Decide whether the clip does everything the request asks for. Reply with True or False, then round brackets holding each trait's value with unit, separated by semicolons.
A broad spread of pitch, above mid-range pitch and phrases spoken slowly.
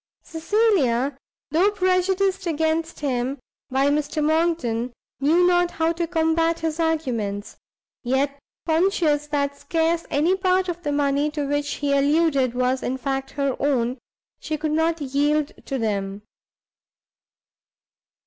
False (3.4 semitones; 300 Hz; 130 wpm)